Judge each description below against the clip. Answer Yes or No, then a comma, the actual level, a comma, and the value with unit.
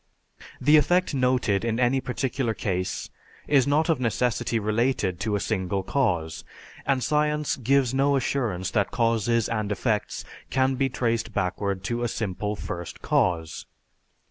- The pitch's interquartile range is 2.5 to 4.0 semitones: No, average, 4.7 semitones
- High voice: No, low, 115 Hz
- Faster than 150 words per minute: No, average, 145 wpm